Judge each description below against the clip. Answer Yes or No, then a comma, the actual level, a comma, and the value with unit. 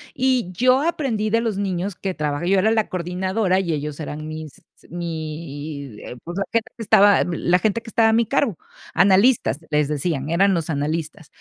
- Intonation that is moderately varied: No, wide, 5.8 semitones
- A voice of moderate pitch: Yes, medium, 180 Hz